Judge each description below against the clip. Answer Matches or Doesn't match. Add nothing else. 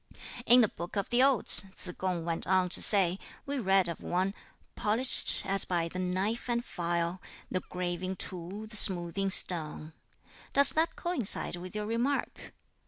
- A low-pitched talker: Doesn't match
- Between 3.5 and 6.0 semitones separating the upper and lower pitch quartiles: Matches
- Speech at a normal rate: Matches